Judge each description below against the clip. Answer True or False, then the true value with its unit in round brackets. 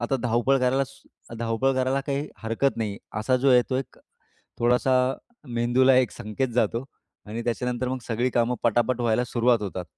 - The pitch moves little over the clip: True (2.0 semitones)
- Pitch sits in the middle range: False (125 Hz)